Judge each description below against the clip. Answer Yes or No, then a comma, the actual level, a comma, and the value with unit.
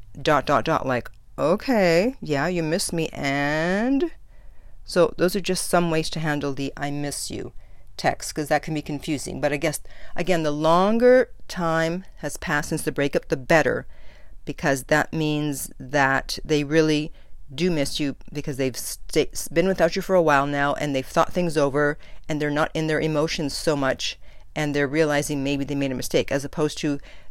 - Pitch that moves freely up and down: No, average, 2.8 semitones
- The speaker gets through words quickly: No, average, 185 wpm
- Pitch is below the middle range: No, medium, 150 Hz